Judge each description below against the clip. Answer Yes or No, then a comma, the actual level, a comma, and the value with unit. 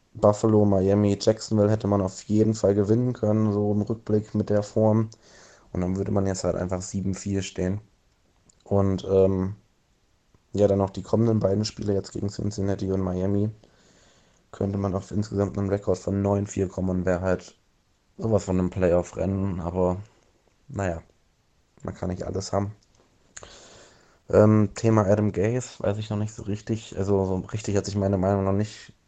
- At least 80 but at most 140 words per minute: No, average, 165 wpm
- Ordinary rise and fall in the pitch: No, narrow, 1.9 semitones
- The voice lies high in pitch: No, low, 100 Hz